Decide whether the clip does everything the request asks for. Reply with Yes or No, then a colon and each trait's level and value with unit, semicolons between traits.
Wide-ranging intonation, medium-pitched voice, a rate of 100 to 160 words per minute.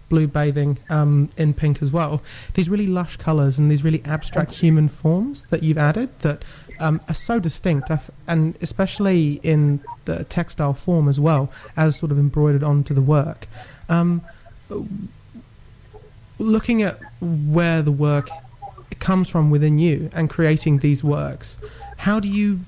No: average, 2.7 semitones; medium, 155 Hz; average, 150 wpm